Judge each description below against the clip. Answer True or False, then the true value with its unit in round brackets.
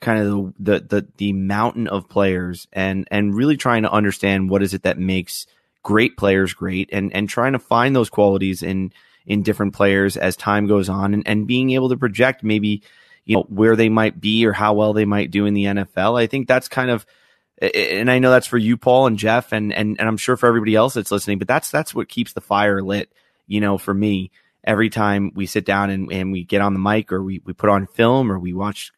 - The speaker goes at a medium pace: False (240 wpm)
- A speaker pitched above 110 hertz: False (105 Hz)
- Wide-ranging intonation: False (2.4 semitones)